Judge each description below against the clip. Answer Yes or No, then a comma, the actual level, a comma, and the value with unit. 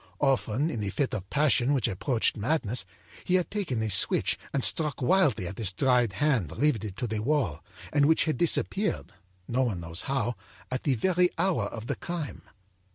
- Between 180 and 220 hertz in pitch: No, low, 130 Hz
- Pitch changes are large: Yes, wide, 5.8 semitones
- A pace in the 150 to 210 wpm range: Yes, average, 185 wpm